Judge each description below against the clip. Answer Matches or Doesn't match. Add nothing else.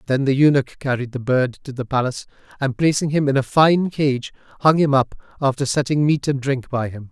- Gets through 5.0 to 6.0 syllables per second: Matches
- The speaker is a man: Matches